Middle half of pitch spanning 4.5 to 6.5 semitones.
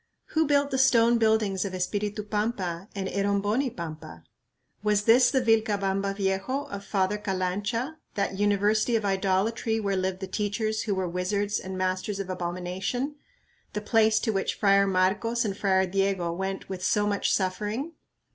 No: narrow, 2.6 semitones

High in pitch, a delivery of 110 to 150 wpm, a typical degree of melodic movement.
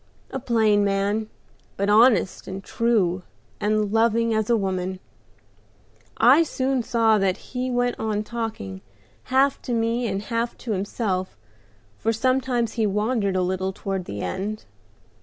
Yes: high, 220 Hz; average, 145 wpm; average, 3.3 semitones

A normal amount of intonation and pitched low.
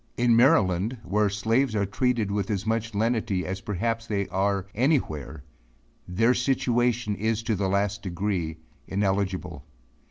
Yes: average, 3.1 semitones; low, 105 Hz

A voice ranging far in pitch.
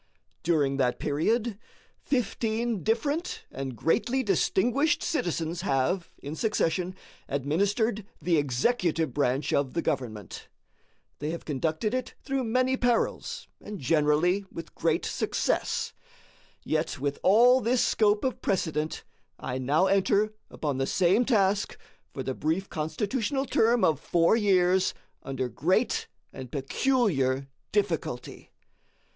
Yes: wide, 7.4 semitones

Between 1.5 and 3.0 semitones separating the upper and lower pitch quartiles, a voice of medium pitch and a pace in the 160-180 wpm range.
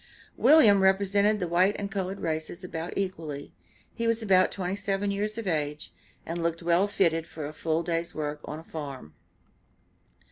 No: average, 3.7 semitones; medium, 180 Hz; average, 170 wpm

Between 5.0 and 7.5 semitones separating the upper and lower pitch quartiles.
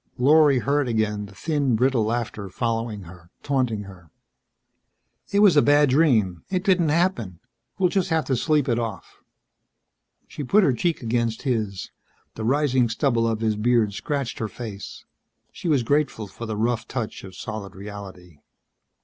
Yes: wide, 5.4 semitones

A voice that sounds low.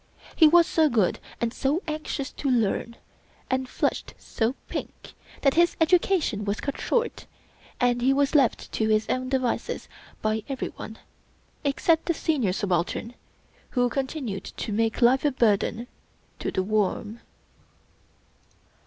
No: very high, 250 Hz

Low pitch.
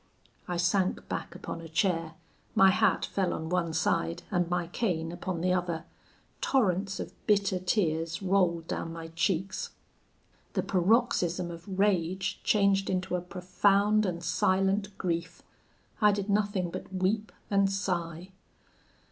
No: medium, 185 Hz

